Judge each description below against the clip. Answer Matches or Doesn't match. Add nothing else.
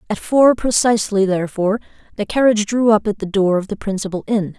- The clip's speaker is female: Matches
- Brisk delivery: Doesn't match